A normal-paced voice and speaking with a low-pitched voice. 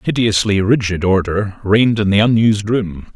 Yes: average, 150 wpm; low, 105 Hz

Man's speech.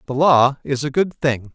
Yes: male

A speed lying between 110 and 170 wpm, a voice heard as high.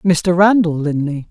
No: average, 140 wpm; medium, 170 Hz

